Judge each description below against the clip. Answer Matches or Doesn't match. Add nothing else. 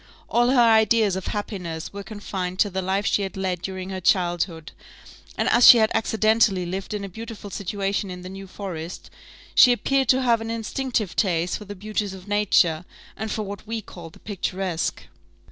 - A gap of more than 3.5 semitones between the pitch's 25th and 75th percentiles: Doesn't match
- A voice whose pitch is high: Matches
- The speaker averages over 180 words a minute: Matches